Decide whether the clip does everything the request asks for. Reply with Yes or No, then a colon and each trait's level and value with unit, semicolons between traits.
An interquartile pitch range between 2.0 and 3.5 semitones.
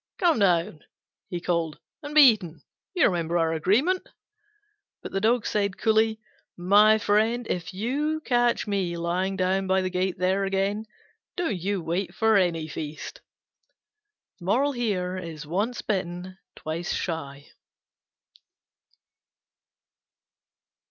No: average, 4.0 semitones